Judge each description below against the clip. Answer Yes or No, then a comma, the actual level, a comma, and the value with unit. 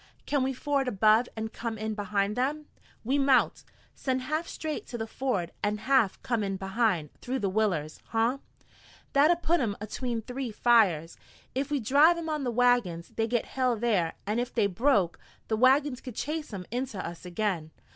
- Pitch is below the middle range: No, high, 235 Hz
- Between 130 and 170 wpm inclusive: No, average, 185 wpm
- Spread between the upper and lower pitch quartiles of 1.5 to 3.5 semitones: No, average, 4.5 semitones